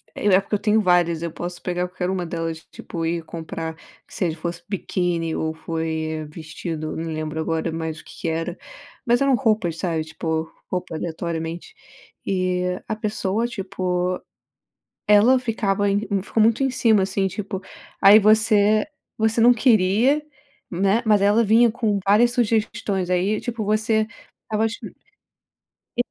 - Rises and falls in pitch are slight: No, average, 4.7 semitones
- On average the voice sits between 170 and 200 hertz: Yes, high, 190 Hz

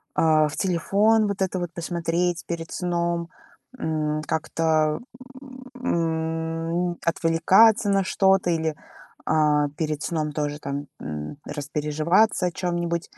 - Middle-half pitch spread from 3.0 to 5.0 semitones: No, narrow, 2.4 semitones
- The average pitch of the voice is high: No, medium, 165 Hz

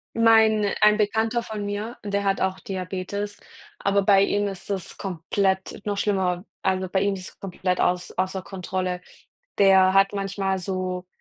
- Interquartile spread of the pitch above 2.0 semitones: No, narrow, 1.6 semitones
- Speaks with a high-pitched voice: Yes, high, 195 Hz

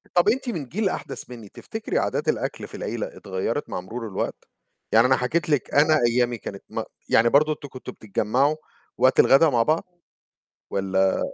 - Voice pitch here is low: Yes, low, 130 Hz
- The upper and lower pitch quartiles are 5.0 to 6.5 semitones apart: Yes, wide, 5.6 semitones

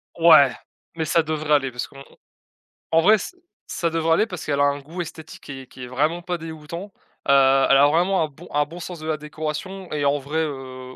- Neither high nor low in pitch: Yes, medium, 155 Hz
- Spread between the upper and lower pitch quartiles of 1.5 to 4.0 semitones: Yes, average, 2.9 semitones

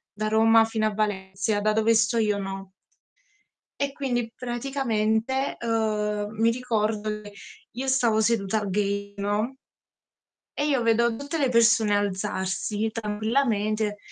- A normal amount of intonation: No, narrow, 2.1 semitones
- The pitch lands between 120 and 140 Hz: No, high, 220 Hz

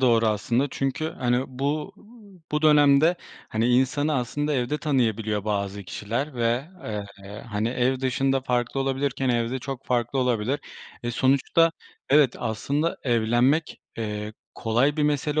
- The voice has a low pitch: Yes, low, 130 Hz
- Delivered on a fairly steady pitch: No, average, 3.4 semitones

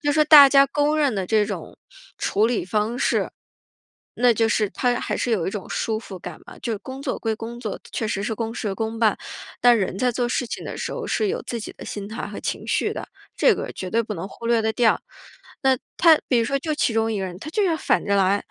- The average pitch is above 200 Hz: Yes, high, 230 Hz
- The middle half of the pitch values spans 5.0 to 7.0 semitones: No, average, 3.7 semitones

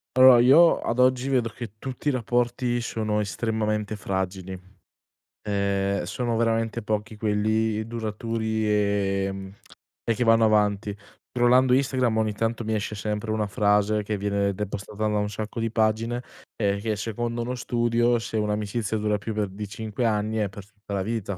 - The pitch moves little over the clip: Yes, narrow, 2.1 semitones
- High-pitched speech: No, low, 110 Hz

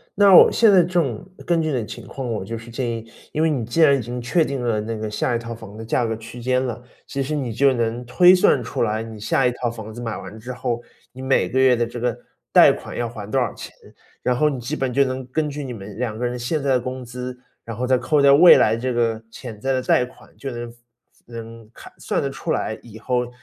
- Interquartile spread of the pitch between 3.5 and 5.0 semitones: No, average, 2.7 semitones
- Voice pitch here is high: No, low, 125 Hz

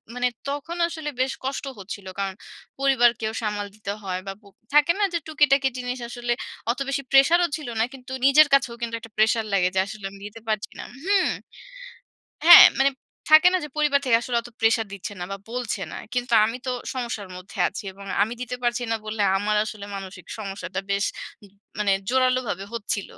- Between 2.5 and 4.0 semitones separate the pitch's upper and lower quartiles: No, average, 4.8 semitones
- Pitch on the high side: Yes, high, 235 Hz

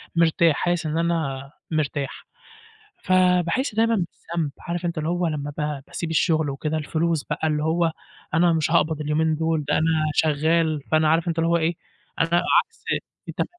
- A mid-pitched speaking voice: Yes, medium, 160 Hz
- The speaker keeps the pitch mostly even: Yes, narrow, 1.8 semitones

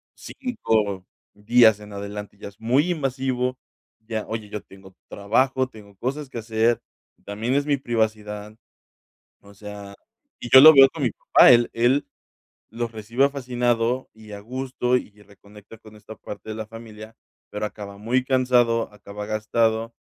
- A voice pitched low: Yes, low, 110 Hz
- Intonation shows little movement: No, average, 3.2 semitones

